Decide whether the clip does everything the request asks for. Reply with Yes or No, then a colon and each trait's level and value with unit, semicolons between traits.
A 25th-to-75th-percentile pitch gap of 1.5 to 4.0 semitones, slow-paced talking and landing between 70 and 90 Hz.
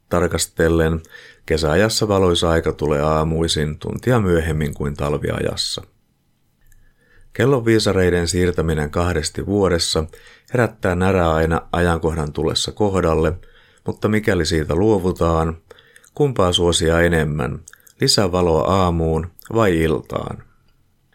Yes: average, 3.3 semitones; slow, 90 wpm; very low, 85 Hz